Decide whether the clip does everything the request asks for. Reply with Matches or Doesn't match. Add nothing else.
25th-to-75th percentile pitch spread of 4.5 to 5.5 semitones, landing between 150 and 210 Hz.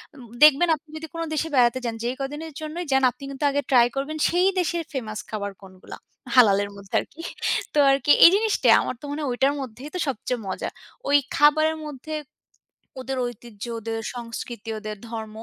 Doesn't match